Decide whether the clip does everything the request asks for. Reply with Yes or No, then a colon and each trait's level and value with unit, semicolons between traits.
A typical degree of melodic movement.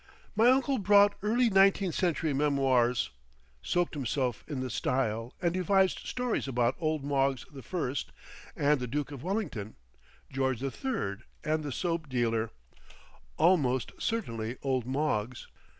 No: wide, 6.5 semitones